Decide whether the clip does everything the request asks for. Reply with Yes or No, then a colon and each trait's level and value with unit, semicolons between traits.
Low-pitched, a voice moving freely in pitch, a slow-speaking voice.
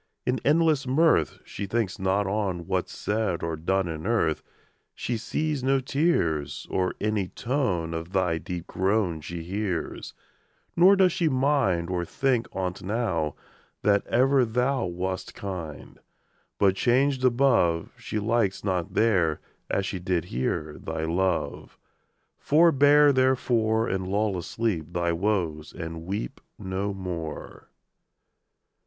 Yes: very low, 95 Hz; wide, 6.3 semitones; slow, 130 wpm